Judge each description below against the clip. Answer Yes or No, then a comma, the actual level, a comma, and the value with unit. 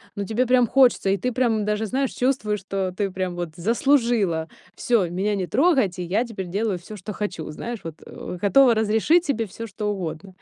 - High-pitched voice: Yes, high, 210 Hz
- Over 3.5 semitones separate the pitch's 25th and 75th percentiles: Yes, average, 4.3 semitones